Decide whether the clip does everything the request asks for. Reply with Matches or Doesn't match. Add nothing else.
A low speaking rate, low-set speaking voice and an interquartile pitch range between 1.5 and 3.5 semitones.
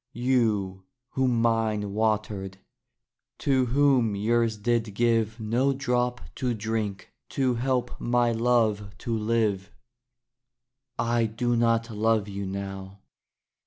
Matches